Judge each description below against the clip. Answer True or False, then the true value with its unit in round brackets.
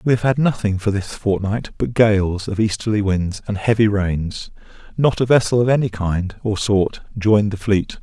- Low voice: True (105 Hz)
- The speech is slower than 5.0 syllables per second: True (4.8 syllables/s)